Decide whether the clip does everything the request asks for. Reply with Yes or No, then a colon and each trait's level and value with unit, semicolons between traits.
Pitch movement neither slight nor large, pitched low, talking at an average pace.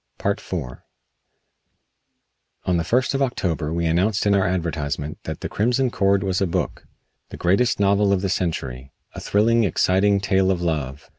Yes: average, 3.5 semitones; very low, 95 Hz; average, 160 wpm